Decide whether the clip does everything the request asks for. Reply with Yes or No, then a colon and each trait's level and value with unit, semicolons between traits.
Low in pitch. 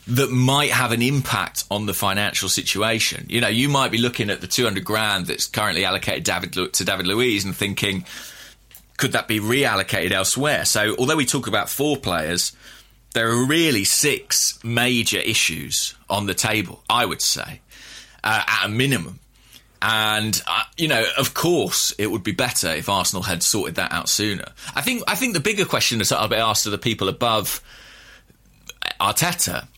Yes: low, 110 Hz